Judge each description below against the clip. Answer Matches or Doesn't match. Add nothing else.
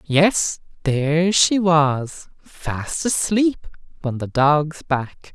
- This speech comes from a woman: Doesn't match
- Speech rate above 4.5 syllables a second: Doesn't match